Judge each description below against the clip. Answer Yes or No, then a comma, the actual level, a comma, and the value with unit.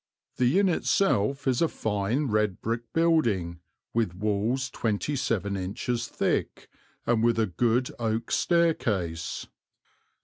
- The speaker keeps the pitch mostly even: No, average, 4.4 semitones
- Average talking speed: No, slow, 125 wpm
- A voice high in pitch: No, low, 115 Hz